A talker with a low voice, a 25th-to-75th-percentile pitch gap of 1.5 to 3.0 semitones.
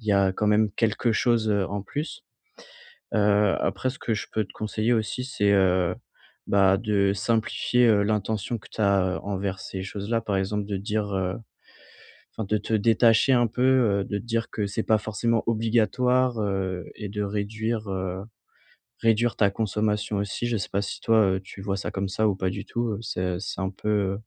Yes: low, 105 Hz; narrow, 2.4 semitones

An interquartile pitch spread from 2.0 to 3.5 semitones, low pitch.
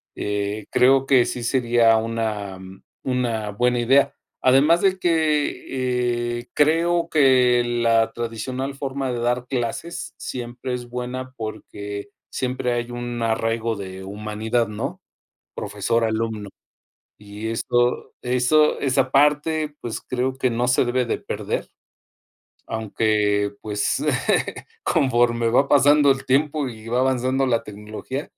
Yes: average, 2.8 semitones; low, 120 Hz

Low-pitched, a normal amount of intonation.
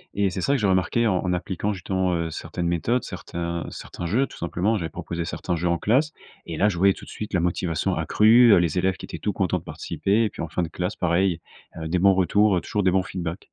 Yes: very low, 90 Hz; average, 3.1 semitones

